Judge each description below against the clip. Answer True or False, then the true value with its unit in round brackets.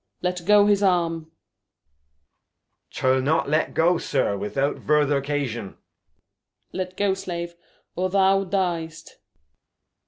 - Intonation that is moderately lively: True (4.4 semitones)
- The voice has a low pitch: False (170 Hz)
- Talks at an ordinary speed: False (120 wpm)